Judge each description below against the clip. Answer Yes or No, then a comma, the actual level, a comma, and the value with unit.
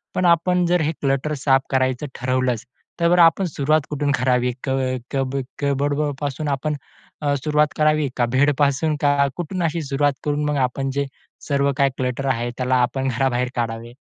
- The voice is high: No, medium, 140 Hz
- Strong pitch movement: No, average, 2.7 semitones